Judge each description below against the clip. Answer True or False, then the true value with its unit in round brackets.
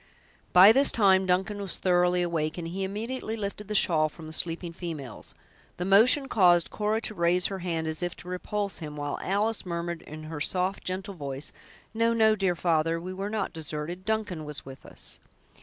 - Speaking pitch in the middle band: True (180 Hz)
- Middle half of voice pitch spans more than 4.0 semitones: False (3.7 semitones)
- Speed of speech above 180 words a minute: True (190 wpm)